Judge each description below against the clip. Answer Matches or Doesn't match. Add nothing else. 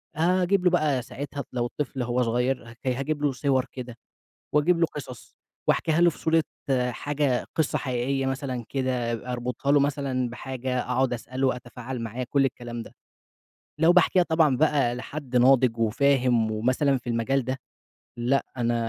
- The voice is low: Matches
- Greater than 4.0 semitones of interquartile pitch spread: Doesn't match